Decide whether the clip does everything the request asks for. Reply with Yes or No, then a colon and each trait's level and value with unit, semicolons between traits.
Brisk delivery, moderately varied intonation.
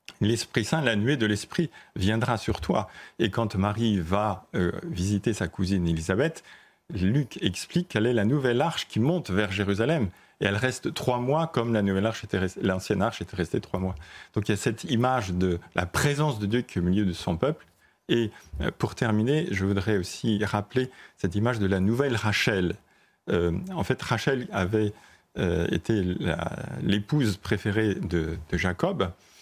No: average, 185 wpm; average, 3.5 semitones